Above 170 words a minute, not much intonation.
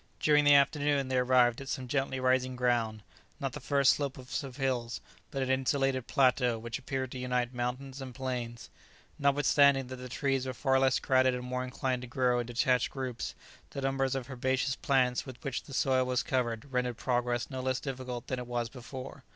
Yes: average, 195 wpm; narrow, 1.4 semitones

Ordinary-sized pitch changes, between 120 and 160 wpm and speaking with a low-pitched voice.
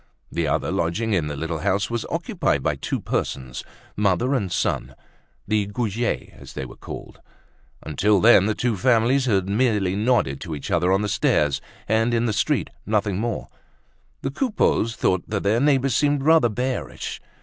No: average, 4.5 semitones; average, 170 wpm; low, 105 Hz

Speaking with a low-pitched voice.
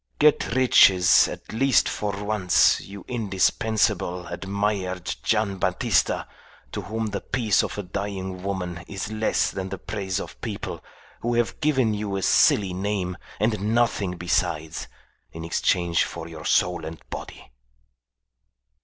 Yes: low, 100 Hz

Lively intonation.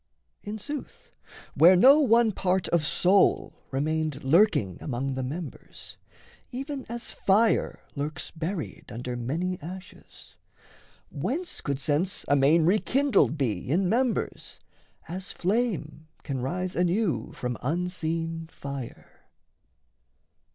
Yes: wide, 6.1 semitones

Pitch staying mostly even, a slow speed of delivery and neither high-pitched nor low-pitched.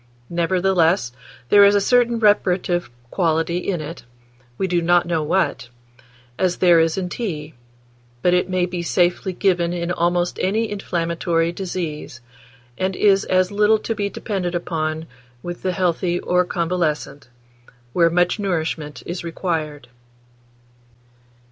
Yes: narrow, 2.2 semitones; slow, 130 wpm; medium, 175 Hz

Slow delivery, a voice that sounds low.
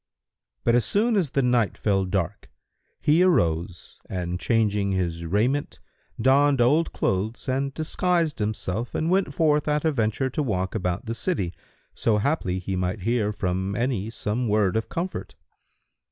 No: average, 155 wpm; low, 115 Hz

